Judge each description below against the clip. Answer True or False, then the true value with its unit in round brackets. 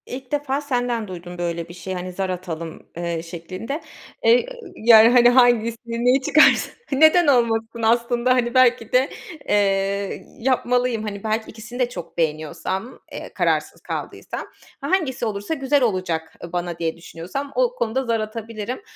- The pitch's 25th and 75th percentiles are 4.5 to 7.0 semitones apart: True (5.4 semitones)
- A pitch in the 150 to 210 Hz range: False (230 Hz)